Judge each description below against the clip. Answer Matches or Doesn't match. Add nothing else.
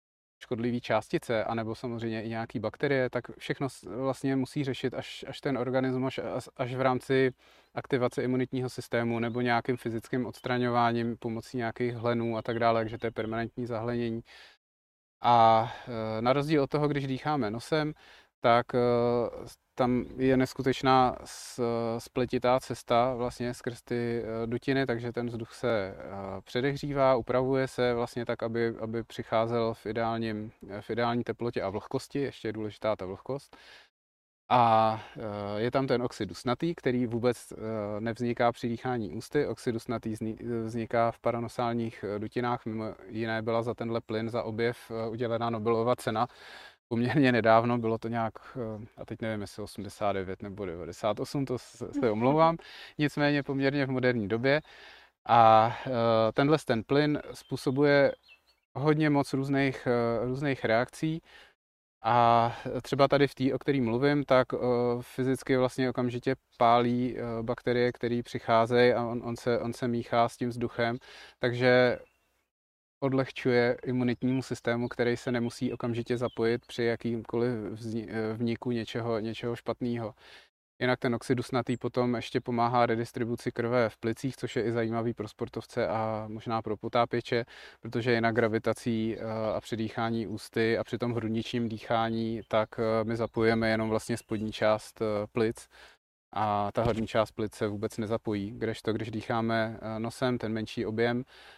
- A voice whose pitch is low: Matches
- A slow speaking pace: Doesn't match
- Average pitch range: Doesn't match